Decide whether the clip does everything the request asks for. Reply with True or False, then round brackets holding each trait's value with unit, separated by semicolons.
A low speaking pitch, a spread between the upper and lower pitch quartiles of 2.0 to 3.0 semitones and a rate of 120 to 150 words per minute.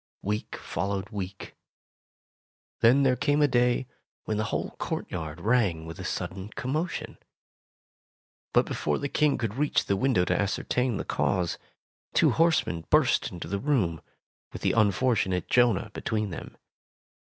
False (110 Hz; 5.4 semitones; 145 wpm)